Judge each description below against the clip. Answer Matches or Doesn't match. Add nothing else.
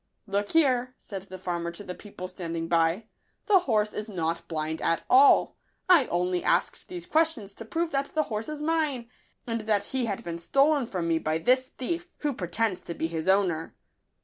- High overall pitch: Matches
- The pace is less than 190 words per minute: Doesn't match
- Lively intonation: Matches